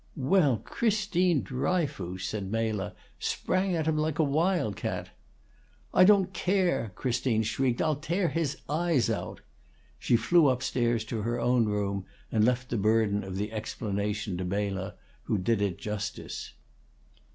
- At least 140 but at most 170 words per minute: Yes, average, 150 wpm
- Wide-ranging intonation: Yes, wide, 7.3 semitones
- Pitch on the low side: Yes, low, 120 Hz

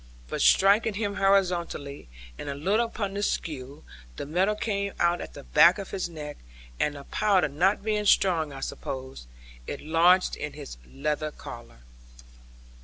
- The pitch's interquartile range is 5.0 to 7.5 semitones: Yes, wide, 5.6 semitones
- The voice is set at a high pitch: No, medium, 175 Hz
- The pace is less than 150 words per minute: No, average, 160 wpm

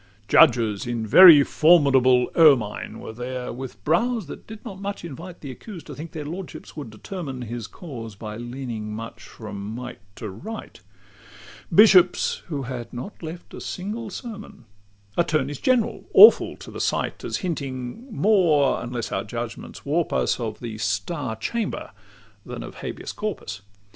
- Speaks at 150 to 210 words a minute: Yes, average, 155 wpm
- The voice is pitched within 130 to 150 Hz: Yes, medium, 140 Hz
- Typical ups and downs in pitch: No, wide, 7.0 semitones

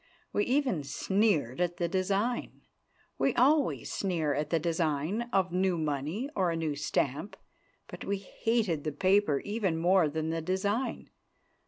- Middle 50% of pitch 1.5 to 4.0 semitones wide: No, average, 4.6 semitones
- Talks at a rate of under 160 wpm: Yes, average, 150 wpm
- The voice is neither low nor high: Yes, medium, 180 Hz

